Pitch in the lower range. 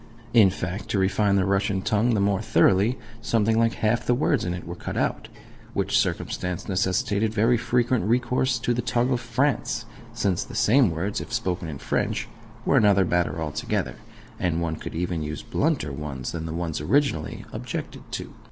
Yes: low, 100 Hz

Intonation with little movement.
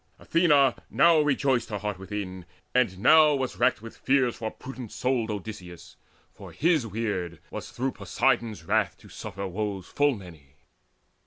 No: wide, 5.4 semitones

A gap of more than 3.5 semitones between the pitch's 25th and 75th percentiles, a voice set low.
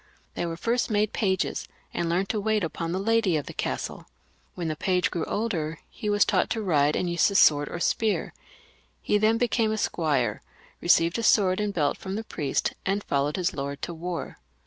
No: average, 4.7 semitones; medium, 185 Hz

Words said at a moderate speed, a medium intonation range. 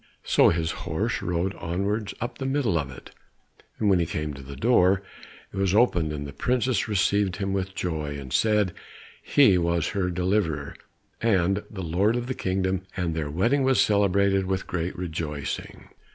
Yes: average, 170 wpm; average, 3.6 semitones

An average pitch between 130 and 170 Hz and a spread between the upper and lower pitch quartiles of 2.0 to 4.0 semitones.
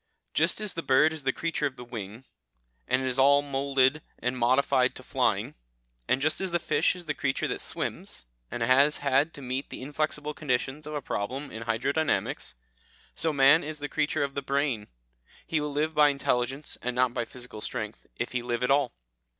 Yes: low, 135 Hz; average, 2.9 semitones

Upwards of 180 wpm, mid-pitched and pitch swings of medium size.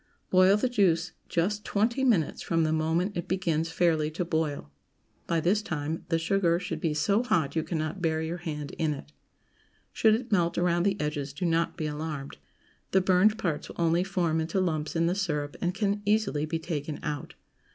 Yes: average, 195 wpm; medium, 170 Hz; average, 3.4 semitones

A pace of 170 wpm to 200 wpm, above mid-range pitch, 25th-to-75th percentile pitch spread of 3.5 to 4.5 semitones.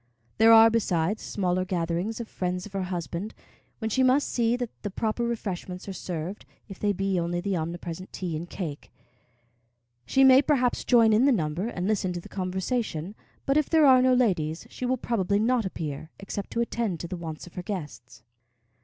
No: average, 195 wpm; high, 195 Hz; average, 4.9 semitones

